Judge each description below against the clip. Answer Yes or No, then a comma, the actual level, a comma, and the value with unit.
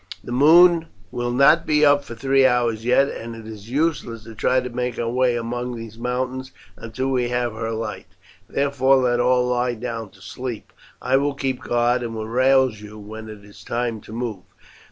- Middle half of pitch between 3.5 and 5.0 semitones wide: No, narrow, 2.4 semitones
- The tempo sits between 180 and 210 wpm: Yes, average, 195 wpm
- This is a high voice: No, low, 120 Hz